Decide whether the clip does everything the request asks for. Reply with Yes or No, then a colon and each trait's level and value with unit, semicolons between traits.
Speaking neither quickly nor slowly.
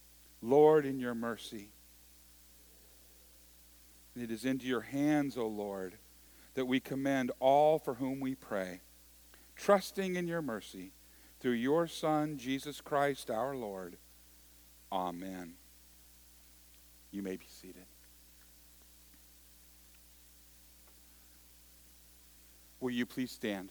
No: slow, 105 wpm